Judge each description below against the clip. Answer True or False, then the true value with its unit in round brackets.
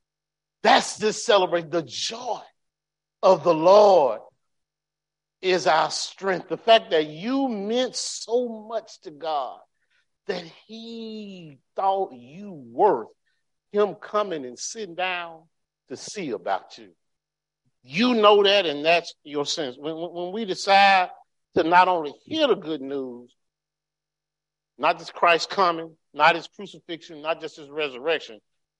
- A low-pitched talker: False (175 Hz)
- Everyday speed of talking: False (130 wpm)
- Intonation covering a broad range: False (4.9 semitones)